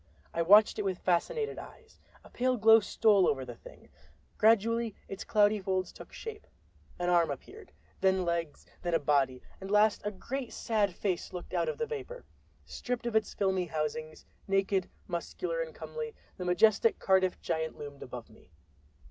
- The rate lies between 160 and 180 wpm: Yes, average, 165 wpm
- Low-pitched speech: No, high, 195 Hz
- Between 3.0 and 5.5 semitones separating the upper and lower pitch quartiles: Yes, average, 4.9 semitones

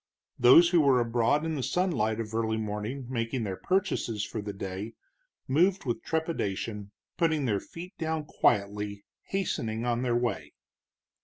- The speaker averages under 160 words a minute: Yes, average, 150 wpm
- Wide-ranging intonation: Yes, wide, 7.0 semitones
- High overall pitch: No, low, 120 Hz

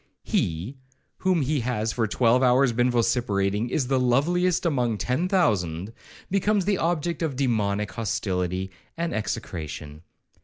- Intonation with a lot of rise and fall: Yes, wide, 6.9 semitones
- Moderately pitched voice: No, low, 120 Hz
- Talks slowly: Yes, slow, 130 wpm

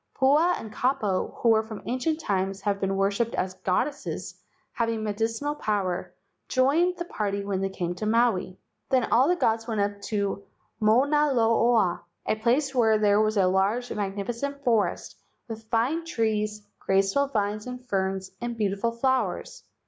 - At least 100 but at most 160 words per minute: Yes, average, 155 wpm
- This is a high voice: Yes, high, 220 Hz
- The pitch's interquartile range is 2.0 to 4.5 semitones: Yes, average, 3.9 semitones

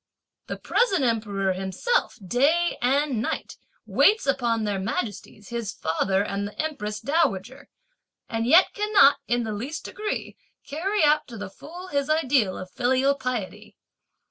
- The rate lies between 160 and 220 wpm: No, average, 145 wpm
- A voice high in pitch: Yes, high, 245 Hz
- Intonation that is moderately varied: No, wide, 6.7 semitones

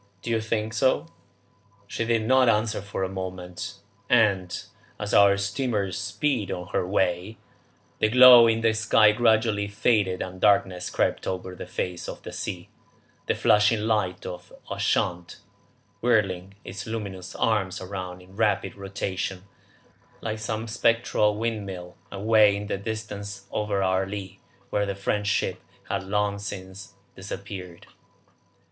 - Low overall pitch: Yes, low, 100 Hz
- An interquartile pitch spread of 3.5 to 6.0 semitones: No, narrow, 2.6 semitones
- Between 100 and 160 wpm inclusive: Yes, average, 140 wpm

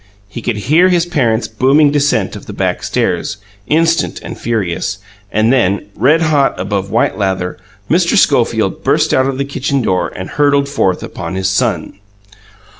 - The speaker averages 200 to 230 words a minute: No, average, 165 wpm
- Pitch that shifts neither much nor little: No, wide, 6.3 semitones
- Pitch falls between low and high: No, low, 130 Hz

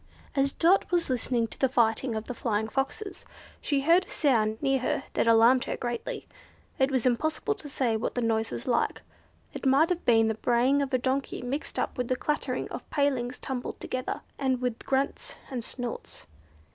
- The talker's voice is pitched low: No, very high, 255 Hz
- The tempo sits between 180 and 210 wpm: Yes, average, 195 wpm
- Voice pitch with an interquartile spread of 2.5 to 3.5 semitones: Yes, average, 2.8 semitones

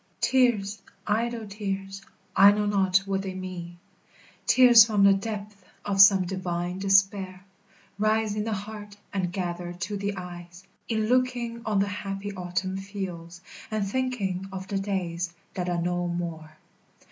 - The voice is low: No, high, 195 Hz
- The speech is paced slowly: No, average, 145 wpm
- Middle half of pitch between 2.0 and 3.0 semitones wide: Yes, narrow, 2.5 semitones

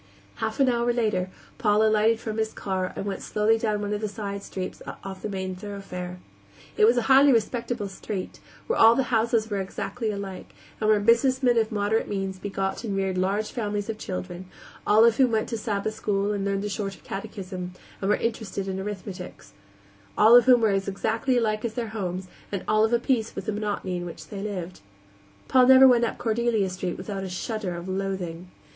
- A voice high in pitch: Yes, high, 210 Hz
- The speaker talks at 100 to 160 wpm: No, average, 200 wpm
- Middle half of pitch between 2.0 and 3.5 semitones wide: Yes, average, 2.7 semitones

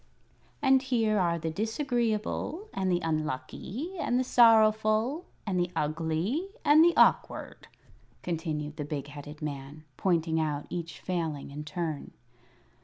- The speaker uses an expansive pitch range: Yes, wide, 6.8 semitones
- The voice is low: No, medium, 175 Hz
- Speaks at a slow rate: Yes, slow, 130 wpm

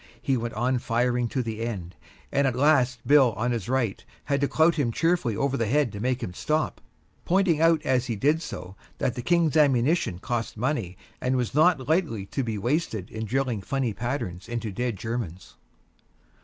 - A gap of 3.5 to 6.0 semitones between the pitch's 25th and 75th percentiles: Yes, average, 4.2 semitones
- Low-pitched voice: Yes, low, 125 Hz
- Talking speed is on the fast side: No, average, 190 wpm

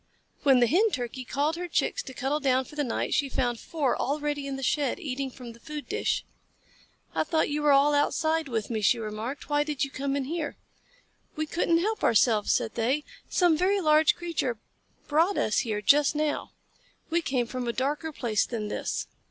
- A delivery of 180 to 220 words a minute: Yes, average, 200 wpm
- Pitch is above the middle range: Yes, very high, 285 Hz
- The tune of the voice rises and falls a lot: No, average, 3.9 semitones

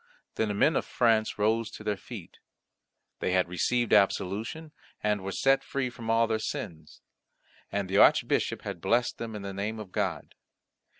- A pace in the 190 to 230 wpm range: No, average, 175 wpm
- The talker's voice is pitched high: No, low, 110 Hz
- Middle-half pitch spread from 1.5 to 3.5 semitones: Yes, average, 2.9 semitones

